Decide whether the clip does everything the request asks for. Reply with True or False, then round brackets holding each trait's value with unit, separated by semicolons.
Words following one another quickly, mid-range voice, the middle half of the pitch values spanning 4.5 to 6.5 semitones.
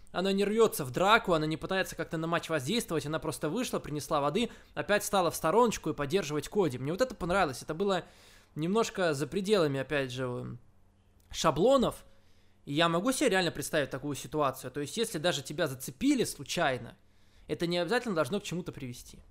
True (180 wpm; 160 Hz; 5.1 semitones)